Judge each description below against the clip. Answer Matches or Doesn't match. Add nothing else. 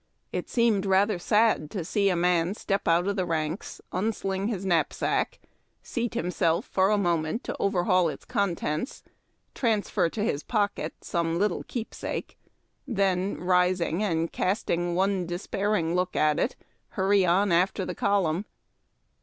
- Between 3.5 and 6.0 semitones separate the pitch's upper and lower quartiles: Doesn't match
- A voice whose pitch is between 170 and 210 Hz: Matches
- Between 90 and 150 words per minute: Matches